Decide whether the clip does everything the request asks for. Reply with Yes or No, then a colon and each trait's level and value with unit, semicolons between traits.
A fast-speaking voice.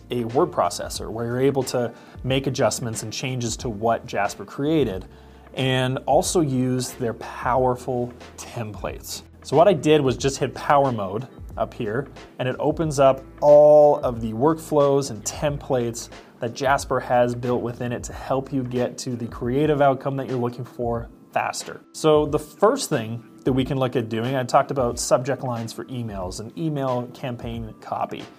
No: average, 175 wpm